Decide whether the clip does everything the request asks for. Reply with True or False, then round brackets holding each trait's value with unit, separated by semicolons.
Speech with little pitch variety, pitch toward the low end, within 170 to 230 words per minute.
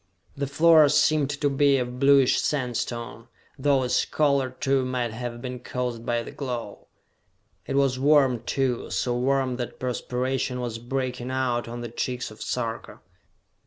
False (2.1 semitones; 125 Hz; 155 wpm)